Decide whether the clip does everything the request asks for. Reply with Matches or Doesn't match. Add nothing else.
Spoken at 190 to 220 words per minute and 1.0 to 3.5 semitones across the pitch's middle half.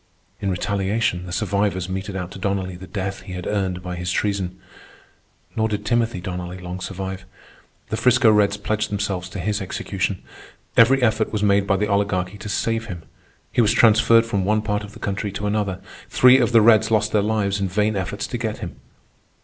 Matches